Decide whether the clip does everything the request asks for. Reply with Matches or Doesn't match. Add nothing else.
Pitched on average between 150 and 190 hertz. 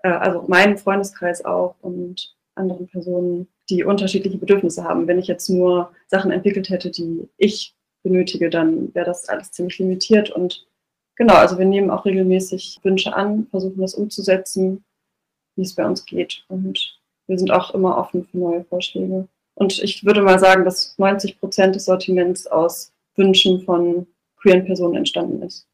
Matches